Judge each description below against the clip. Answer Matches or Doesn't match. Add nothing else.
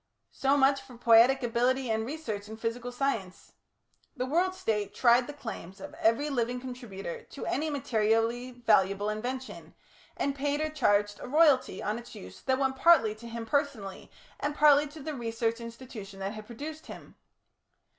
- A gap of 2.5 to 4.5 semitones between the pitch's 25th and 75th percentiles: Matches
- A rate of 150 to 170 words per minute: Matches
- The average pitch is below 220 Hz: Doesn't match